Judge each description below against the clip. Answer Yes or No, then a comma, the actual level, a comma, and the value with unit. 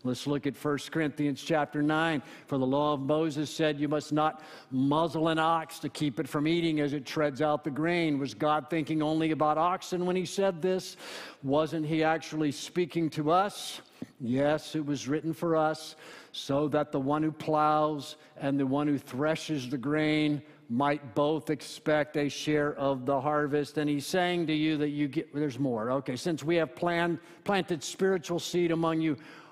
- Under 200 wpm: Yes, average, 190 wpm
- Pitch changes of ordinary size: No, narrow, 1.7 semitones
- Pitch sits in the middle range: Yes, medium, 155 Hz